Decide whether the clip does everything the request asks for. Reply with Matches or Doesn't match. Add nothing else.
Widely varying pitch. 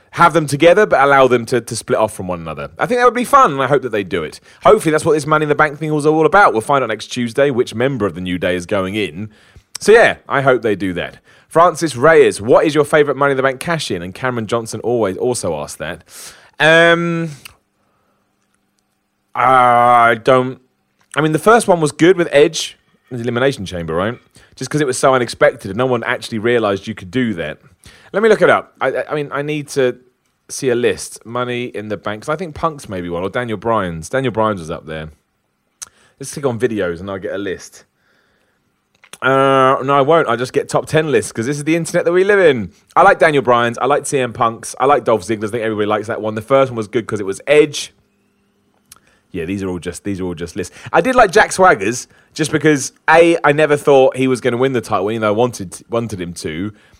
Matches